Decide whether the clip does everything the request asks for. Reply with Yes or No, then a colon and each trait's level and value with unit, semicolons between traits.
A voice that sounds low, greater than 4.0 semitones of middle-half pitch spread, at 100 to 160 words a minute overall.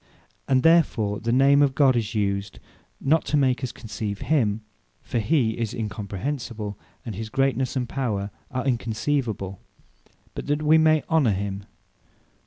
Yes: low, 120 Hz; average, 4.9 semitones; average, 150 wpm